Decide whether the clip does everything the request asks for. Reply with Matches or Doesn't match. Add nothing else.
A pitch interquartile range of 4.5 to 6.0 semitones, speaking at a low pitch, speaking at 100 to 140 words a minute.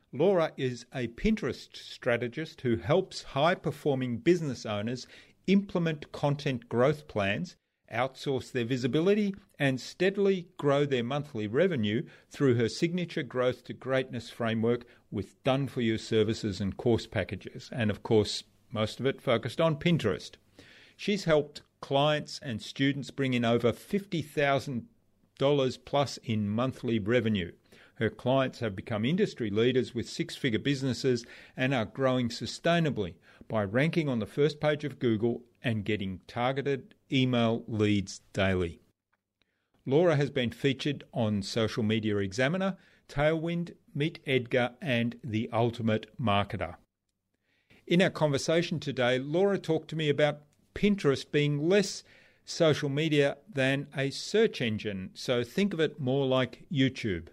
Matches